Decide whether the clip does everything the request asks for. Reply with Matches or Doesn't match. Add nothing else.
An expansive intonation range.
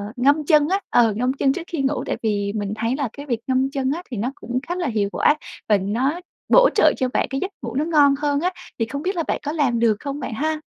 Doesn't match